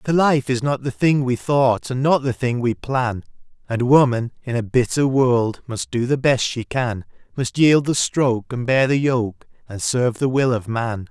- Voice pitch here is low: Yes, low, 125 Hz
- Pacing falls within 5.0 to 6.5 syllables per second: No, 4.4 syllables/s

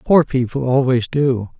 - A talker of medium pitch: No, low, 130 Hz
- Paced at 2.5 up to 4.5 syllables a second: Yes, 4.3 syllables/s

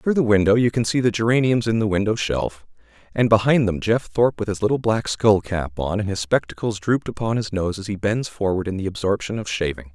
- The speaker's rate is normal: No, fast, 240 wpm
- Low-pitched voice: Yes, low, 105 Hz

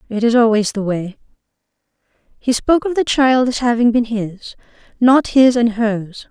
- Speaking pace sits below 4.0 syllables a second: No, 4.5 syllables/s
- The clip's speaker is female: Yes, female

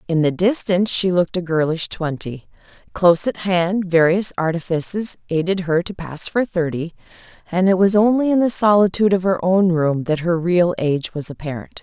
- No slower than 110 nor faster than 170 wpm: No, average, 185 wpm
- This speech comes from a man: No, female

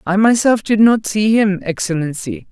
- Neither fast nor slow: Yes, average, 165 wpm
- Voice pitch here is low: No, high, 205 Hz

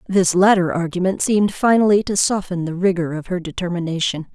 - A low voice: No, medium, 185 Hz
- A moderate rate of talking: Yes, average, 165 wpm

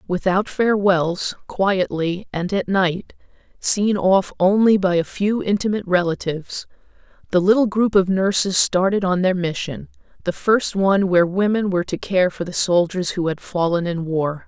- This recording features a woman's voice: Yes, female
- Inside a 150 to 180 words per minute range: Yes, average, 160 wpm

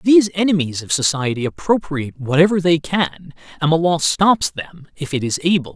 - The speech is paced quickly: No, average, 175 wpm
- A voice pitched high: No, medium, 160 Hz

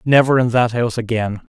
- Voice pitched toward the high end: No, low, 120 Hz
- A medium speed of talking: Yes, average, 195 wpm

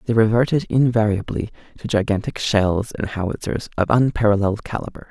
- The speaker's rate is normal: No, slow, 130 wpm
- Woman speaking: No, male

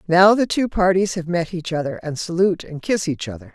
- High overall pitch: No, medium, 175 Hz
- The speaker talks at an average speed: No, fast, 235 wpm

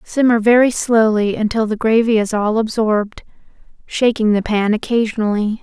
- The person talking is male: No, female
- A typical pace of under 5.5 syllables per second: Yes, 5.1 syllables/s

